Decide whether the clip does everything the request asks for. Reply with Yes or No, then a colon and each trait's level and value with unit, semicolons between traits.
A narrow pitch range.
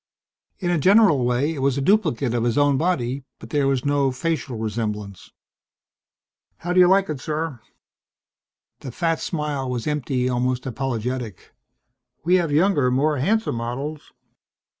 No: average, 4.4 semitones